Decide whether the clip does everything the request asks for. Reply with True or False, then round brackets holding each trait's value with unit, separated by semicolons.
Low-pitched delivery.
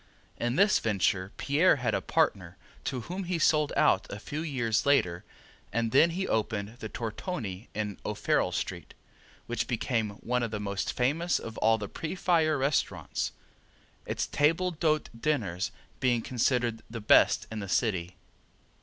True (120 Hz)